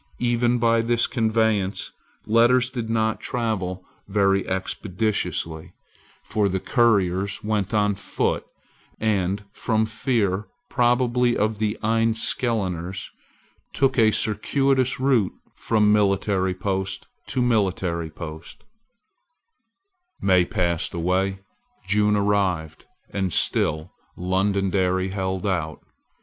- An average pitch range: Yes, average, 3.4 semitones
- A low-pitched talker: Yes, low, 105 Hz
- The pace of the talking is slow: Yes, slow, 100 wpm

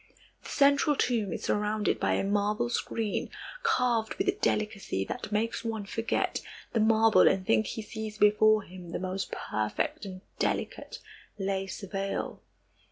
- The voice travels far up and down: No, narrow, 2.5 semitones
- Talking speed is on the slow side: No, average, 150 wpm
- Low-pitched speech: No, high, 210 Hz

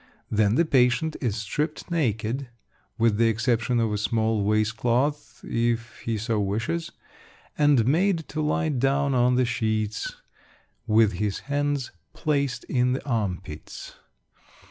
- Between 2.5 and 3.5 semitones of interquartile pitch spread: No, average, 4.4 semitones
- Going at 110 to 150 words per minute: Yes, average, 140 wpm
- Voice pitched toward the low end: Yes, low, 120 Hz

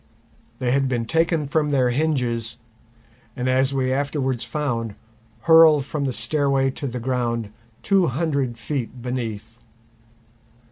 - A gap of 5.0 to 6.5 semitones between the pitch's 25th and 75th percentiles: No, average, 3.4 semitones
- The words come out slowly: Yes, slow, 130 wpm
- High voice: No, low, 130 Hz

